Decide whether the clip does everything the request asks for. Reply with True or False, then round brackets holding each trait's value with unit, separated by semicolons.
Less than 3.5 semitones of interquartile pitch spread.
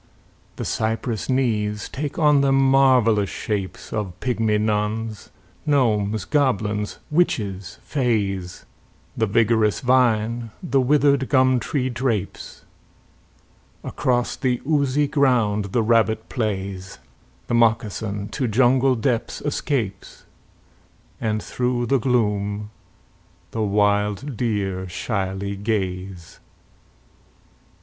False (4.0 semitones)